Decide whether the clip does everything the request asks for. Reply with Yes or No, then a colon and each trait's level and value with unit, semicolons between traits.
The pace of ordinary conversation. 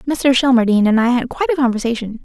No: fast, 215 wpm